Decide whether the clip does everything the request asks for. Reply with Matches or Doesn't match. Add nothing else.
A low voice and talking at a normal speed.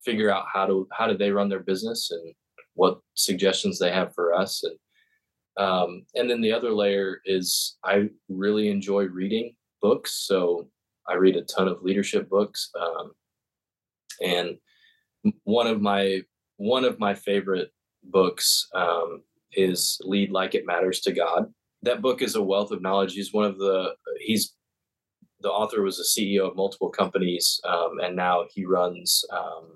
Matches